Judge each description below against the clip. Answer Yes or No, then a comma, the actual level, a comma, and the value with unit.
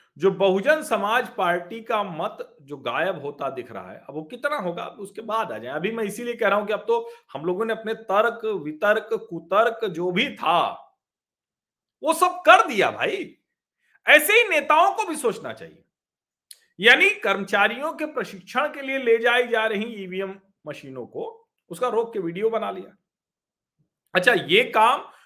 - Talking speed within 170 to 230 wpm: Yes, average, 175 wpm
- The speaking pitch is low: No, high, 220 Hz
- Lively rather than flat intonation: Yes, wide, 7.1 semitones